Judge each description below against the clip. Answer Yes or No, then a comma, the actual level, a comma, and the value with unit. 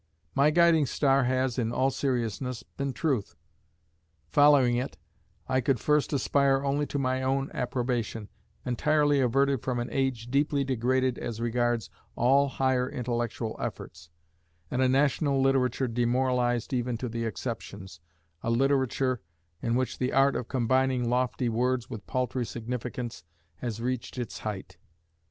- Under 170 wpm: Yes, average, 140 wpm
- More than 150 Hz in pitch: No, low, 125 Hz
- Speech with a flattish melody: Yes, narrow, 2.2 semitones